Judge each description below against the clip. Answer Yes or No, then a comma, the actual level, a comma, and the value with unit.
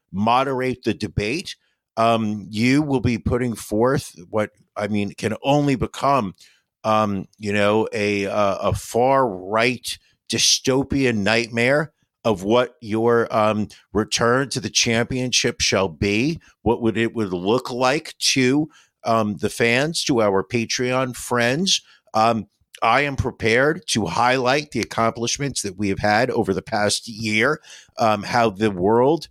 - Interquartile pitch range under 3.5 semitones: Yes, average, 3.1 semitones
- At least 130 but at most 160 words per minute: Yes, average, 140 wpm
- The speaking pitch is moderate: No, low, 115 Hz